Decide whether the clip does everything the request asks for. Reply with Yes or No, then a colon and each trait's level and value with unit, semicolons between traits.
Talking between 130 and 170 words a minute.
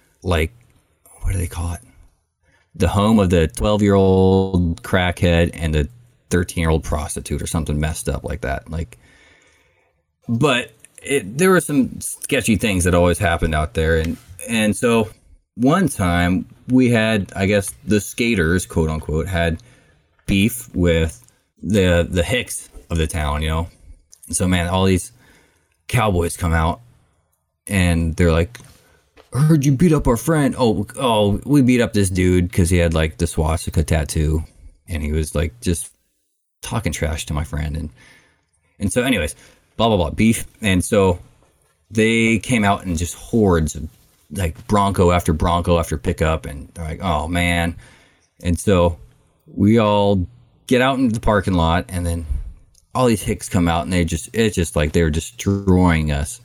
Yes: average, 165 wpm